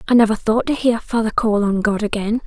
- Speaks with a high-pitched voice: Yes, high, 220 Hz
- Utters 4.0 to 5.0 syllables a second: No, 5.7 syllables/s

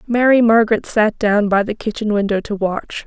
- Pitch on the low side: No, high, 215 Hz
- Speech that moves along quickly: No, average, 195 wpm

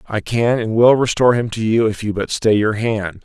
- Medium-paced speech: No, fast, 260 wpm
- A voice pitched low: Yes, low, 110 Hz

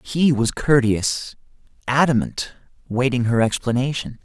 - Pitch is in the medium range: No, low, 125 Hz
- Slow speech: Yes, slow, 100 wpm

